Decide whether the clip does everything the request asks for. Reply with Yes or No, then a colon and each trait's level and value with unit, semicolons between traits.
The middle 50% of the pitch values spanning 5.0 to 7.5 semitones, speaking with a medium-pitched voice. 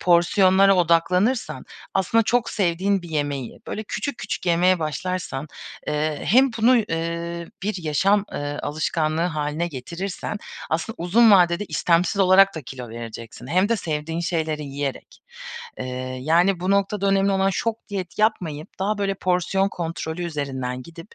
No: average, 3.9 semitones; medium, 175 Hz